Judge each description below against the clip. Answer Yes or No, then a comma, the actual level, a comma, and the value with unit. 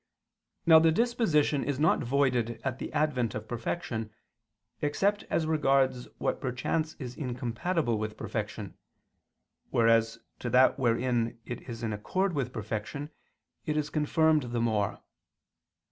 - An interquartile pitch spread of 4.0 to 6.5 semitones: Yes, average, 4.7 semitones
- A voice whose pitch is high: No, low, 130 Hz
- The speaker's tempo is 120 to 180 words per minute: Yes, slow, 135 wpm